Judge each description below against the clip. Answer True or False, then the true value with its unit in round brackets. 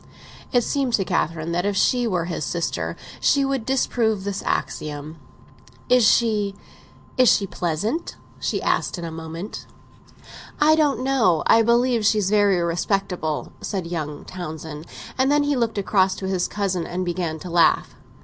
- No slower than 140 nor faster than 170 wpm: True (150 wpm)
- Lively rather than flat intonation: True (5.8 semitones)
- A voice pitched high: True (195 Hz)